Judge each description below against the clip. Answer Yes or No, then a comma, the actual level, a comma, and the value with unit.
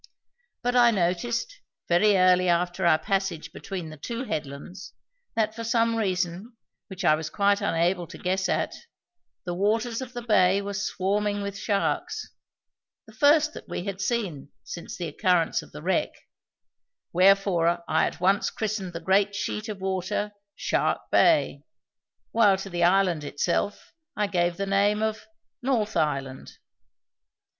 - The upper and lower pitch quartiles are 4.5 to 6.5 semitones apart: No, average, 3.4 semitones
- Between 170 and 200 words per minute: No, average, 150 wpm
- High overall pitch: Yes, high, 195 Hz